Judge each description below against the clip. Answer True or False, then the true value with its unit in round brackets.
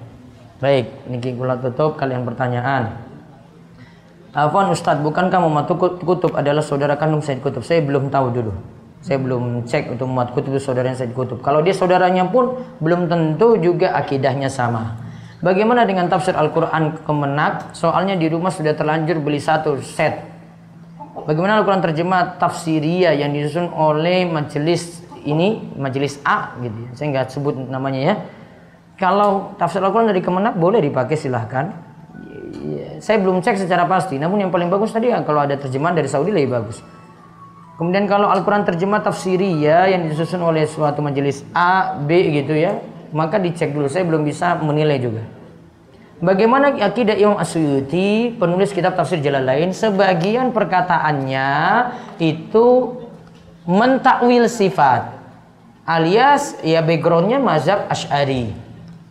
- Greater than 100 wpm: True (140 wpm)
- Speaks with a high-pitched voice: False (165 Hz)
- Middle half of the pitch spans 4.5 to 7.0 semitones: True (4.8 semitones)